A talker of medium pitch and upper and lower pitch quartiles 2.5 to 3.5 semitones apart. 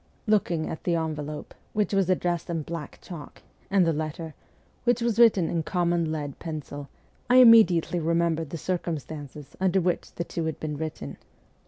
Yes: medium, 165 Hz; average, 2.8 semitones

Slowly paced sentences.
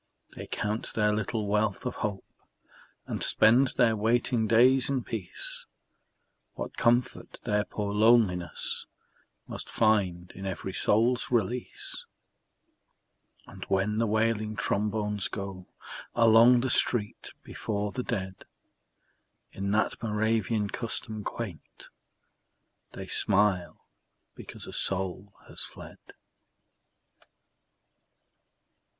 Yes: slow, 100 wpm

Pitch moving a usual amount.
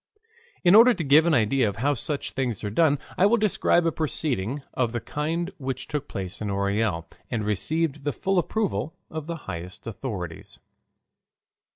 No: wide, 7.5 semitones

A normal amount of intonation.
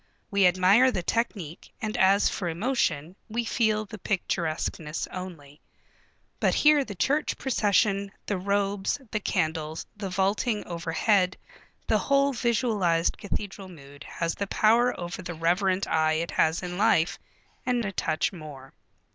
Yes: average, 4.2 semitones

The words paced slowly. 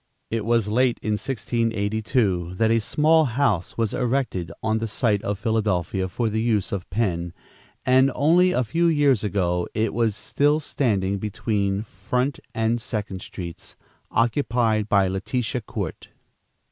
No: average, 145 wpm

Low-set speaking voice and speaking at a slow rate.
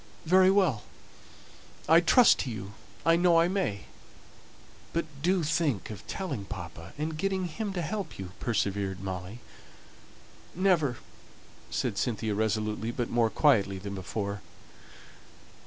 Yes: low, 125 Hz; slow, 125 wpm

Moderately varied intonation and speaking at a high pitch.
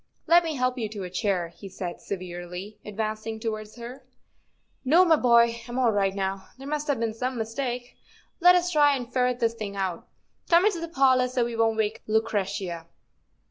Yes: average, 4.4 semitones; high, 230 Hz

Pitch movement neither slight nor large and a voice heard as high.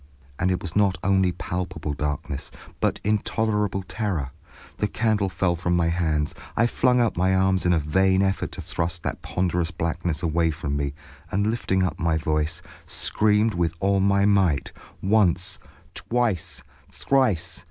No: average, 3.2 semitones; very low, 90 Hz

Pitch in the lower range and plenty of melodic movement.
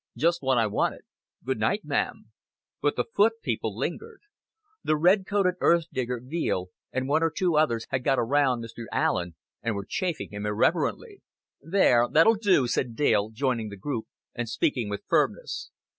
Yes: low, 130 Hz; wide, 6.9 semitones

